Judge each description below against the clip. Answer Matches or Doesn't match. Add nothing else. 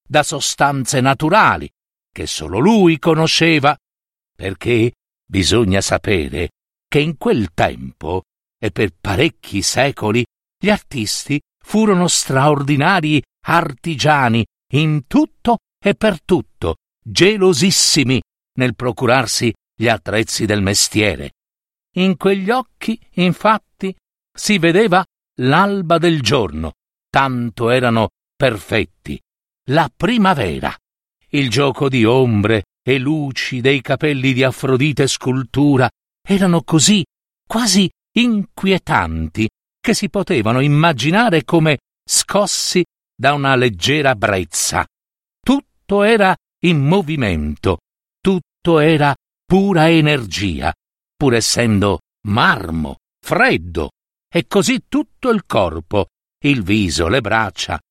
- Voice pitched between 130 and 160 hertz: Matches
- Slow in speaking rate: Matches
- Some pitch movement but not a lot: Doesn't match